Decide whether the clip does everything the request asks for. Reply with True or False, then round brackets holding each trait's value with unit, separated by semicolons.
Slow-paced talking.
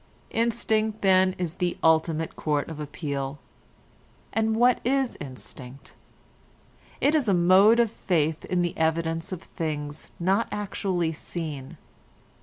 True (125 wpm)